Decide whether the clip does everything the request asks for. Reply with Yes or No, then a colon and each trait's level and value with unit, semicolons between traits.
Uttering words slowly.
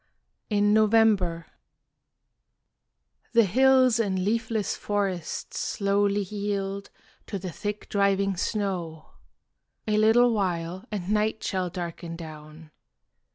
Yes: slow, 100 wpm